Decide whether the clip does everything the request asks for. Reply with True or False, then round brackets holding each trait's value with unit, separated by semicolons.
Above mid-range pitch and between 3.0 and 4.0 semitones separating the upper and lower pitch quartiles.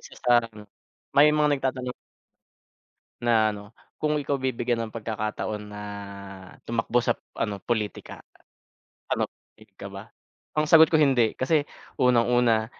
False (120 Hz; 3.7 semitones)